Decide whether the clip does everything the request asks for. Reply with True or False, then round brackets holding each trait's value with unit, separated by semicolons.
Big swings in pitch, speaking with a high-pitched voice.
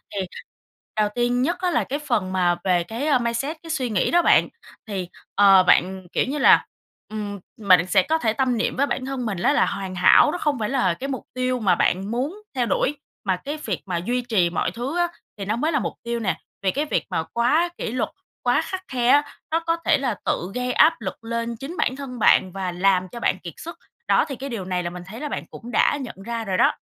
True (6.3 semitones; 235 Hz)